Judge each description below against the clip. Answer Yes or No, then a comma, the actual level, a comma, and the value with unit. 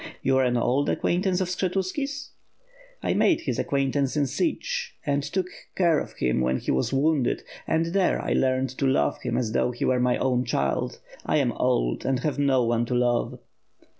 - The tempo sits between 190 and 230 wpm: Yes, average, 195 wpm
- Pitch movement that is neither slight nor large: No, wide, 6.3 semitones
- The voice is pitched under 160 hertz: Yes, low, 135 Hz